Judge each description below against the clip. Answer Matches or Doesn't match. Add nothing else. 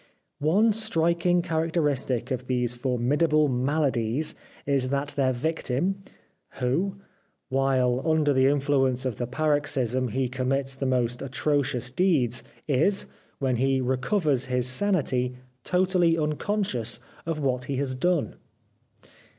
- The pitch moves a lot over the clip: Doesn't match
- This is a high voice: Doesn't match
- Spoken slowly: Matches